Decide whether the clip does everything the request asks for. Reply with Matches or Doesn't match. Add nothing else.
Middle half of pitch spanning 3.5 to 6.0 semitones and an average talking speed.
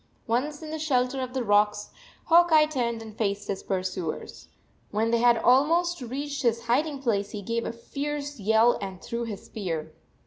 Matches